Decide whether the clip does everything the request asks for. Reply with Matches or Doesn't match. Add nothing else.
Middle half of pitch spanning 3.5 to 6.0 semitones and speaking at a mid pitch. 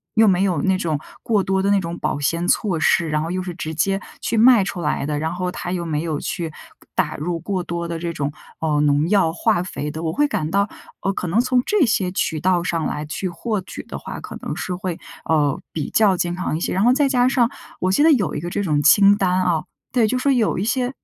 Matches